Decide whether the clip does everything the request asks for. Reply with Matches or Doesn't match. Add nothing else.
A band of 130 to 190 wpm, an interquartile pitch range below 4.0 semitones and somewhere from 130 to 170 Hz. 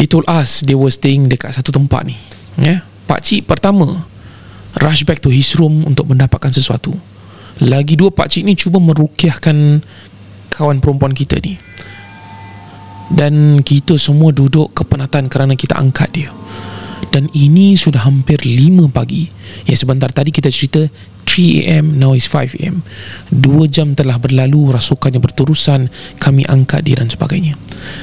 Matches